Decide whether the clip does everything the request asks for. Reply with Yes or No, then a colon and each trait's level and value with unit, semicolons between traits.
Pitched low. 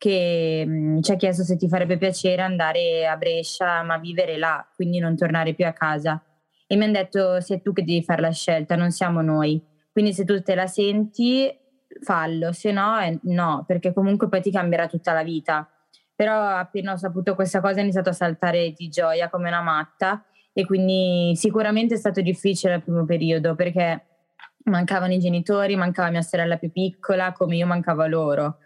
No: medium, 180 Hz